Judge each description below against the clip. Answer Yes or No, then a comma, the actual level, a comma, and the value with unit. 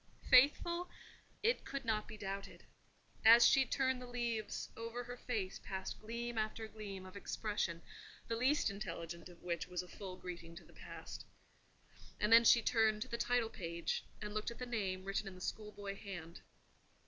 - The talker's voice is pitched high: Yes, high, 215 Hz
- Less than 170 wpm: No, average, 175 wpm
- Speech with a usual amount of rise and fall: Yes, average, 3.8 semitones